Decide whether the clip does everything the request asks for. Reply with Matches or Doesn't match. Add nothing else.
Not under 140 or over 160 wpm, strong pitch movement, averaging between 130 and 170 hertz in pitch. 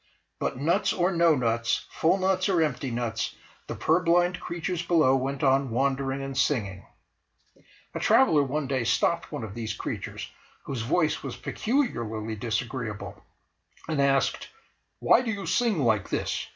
Matches